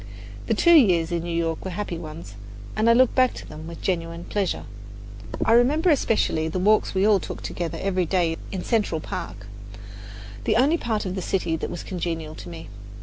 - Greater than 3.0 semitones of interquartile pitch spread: Yes, average, 4.7 semitones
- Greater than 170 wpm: Yes, average, 200 wpm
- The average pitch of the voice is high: No, medium, 180 Hz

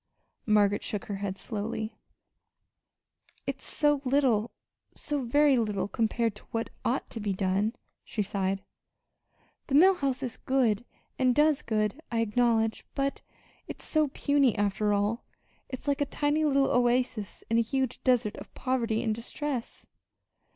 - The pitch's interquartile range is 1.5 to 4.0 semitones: No, average, 4.4 semitones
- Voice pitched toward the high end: Yes, high, 235 Hz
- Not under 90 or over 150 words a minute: Yes, average, 145 wpm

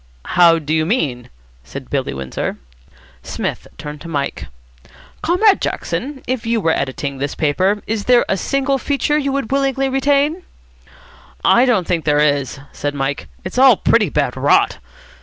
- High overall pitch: Yes, high, 200 Hz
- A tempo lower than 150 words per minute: No, average, 160 wpm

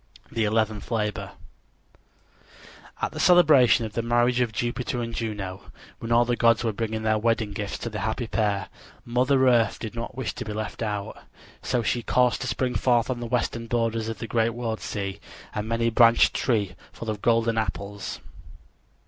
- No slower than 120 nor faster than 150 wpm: No, average, 180 wpm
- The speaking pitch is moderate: No, low, 115 Hz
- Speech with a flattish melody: Yes, narrow, 1.8 semitones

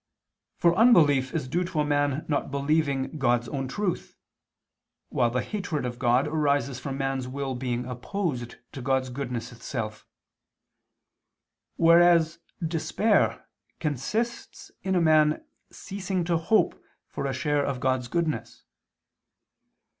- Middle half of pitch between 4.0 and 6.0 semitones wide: Yes, average, 4.5 semitones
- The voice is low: No, medium, 145 Hz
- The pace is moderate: No, slow, 125 wpm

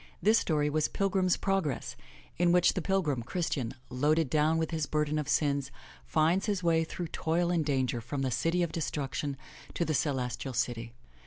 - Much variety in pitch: No, average, 4.0 semitones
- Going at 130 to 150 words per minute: No, average, 185 wpm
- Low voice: No, medium, 155 Hz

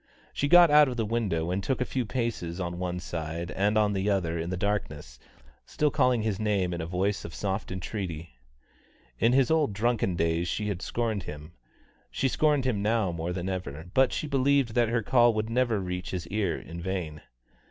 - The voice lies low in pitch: Yes, low, 100 Hz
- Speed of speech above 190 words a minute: Yes, fast, 205 wpm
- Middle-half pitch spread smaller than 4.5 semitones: No, average, 5.2 semitones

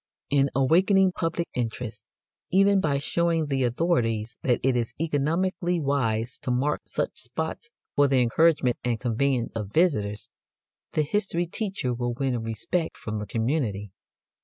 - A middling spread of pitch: No, wide, 6.0 semitones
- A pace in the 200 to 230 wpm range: No, average, 140 wpm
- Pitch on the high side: No, low, 135 Hz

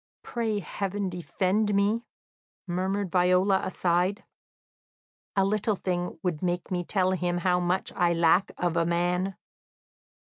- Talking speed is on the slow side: Yes, slow, 130 wpm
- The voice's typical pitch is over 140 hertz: Yes, medium, 185 Hz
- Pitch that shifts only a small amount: Yes, narrow, 1.9 semitones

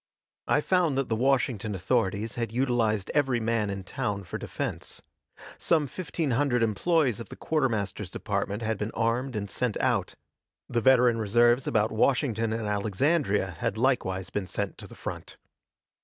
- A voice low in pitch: Yes, low, 115 Hz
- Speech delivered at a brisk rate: No, average, 155 wpm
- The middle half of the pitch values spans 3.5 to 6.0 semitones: Yes, average, 4.2 semitones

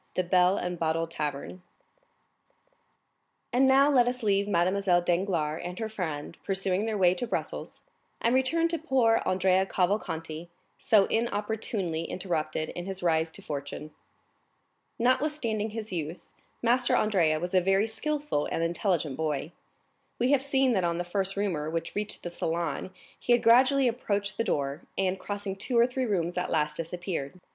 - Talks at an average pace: Yes, average, 160 wpm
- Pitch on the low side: No, high, 190 Hz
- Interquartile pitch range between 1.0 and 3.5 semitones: No, average, 5.2 semitones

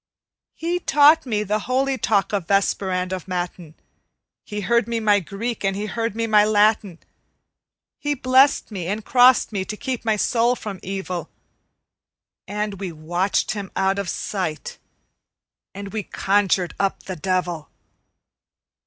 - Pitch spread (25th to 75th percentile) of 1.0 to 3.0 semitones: No, average, 3.4 semitones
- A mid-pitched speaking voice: No, high, 205 Hz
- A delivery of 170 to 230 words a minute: No, average, 150 wpm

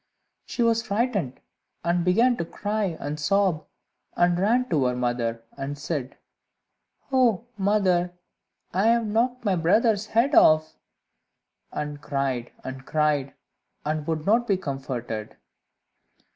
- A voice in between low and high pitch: Yes, medium, 175 Hz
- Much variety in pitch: Yes, wide, 7.0 semitones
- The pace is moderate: No, slow, 125 wpm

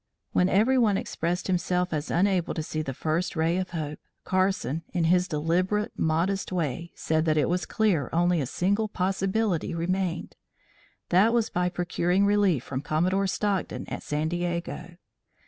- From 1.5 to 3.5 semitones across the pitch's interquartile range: Yes, average, 2.9 semitones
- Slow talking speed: No, average, 160 wpm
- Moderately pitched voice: Yes, medium, 180 Hz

